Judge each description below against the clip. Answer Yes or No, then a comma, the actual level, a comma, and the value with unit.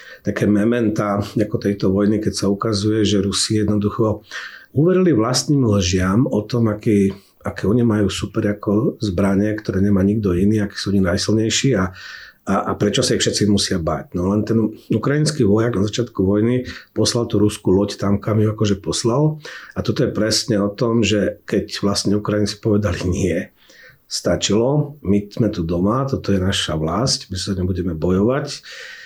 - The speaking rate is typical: No, fast, 170 wpm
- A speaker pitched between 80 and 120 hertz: Yes, low, 105 Hz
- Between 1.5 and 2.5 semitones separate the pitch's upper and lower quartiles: Yes, narrow, 2.2 semitones